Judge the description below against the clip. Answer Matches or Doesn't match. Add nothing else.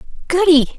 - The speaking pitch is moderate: Doesn't match